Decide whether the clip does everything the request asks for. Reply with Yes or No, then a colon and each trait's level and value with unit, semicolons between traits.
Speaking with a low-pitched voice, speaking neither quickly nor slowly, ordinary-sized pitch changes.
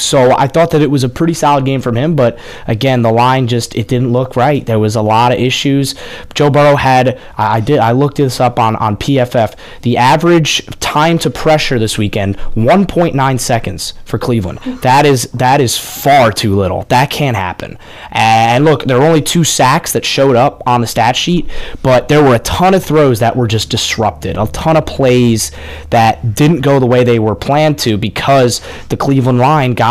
No: low, 125 Hz; fast, 210 wpm; average, 4.1 semitones